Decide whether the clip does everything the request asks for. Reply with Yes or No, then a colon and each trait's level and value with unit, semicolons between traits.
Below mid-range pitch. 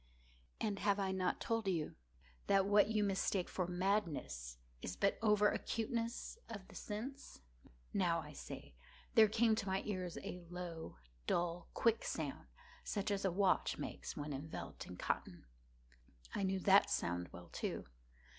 No: high, 190 Hz